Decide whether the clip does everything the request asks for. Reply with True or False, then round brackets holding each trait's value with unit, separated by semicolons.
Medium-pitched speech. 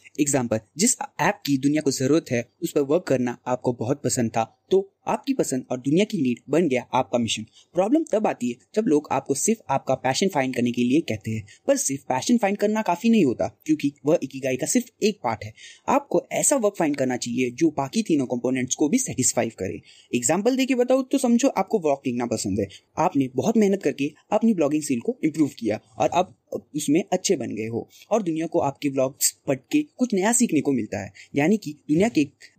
True (150 Hz)